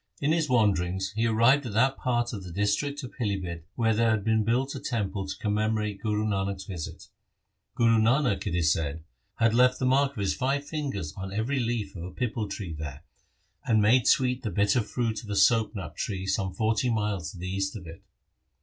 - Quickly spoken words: Yes, fast, 210 wpm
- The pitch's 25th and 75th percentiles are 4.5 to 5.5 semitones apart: No, average, 3.8 semitones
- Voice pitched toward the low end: Yes, low, 110 Hz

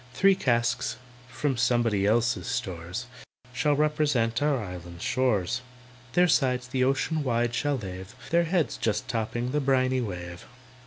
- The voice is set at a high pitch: No, low, 125 Hz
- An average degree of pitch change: Yes, average, 4.0 semitones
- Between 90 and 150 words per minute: Yes, average, 140 wpm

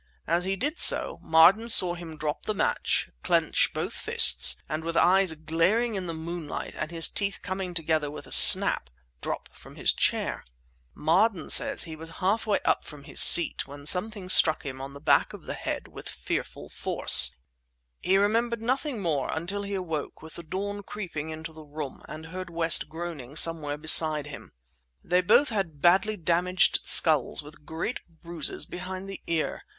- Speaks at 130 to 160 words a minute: No, average, 175 wpm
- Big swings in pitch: No, average, 3.7 semitones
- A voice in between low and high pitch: Yes, medium, 170 Hz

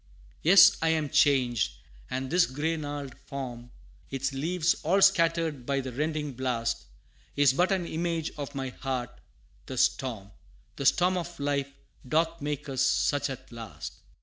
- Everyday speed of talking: Yes, average, 150 wpm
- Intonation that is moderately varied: Yes, average, 3.9 semitones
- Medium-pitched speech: Yes, medium, 145 Hz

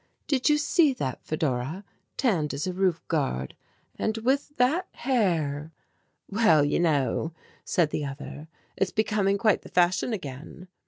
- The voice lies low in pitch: No, medium, 180 Hz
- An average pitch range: No, wide, 7.2 semitones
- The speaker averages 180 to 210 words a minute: No, average, 145 wpm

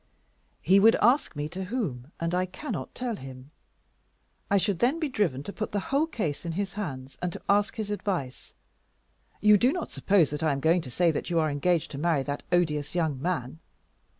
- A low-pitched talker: No, medium, 175 Hz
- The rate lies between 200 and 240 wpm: Yes, fast, 205 wpm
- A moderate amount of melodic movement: No, wide, 5.9 semitones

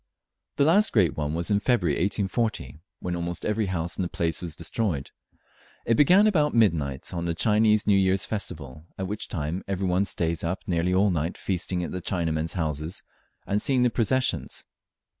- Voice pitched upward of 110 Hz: No, very low, 90 Hz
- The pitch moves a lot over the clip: No, average, 4.3 semitones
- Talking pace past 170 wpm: Yes, average, 180 wpm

